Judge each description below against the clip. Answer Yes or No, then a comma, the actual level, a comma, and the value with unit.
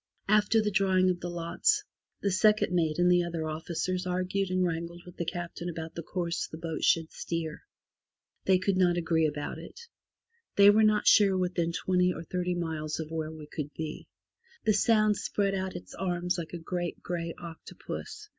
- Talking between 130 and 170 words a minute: No, average, 185 wpm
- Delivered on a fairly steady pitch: Yes, narrow, 2.3 semitones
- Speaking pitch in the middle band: Yes, medium, 175 Hz